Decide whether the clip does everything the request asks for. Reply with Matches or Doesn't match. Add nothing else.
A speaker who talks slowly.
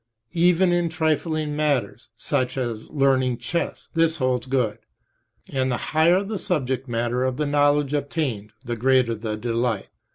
Doesn't match